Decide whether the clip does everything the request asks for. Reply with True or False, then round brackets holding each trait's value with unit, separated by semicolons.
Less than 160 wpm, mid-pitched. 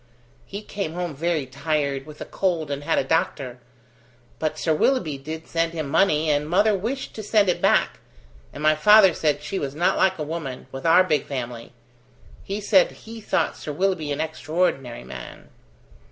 False (180 wpm; 160 Hz)